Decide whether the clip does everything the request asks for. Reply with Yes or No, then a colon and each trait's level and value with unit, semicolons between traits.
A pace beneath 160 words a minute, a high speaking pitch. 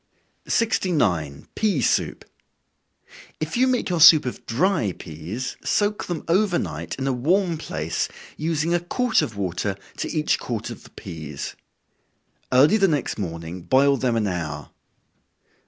No: average, 145 wpm; low, 135 Hz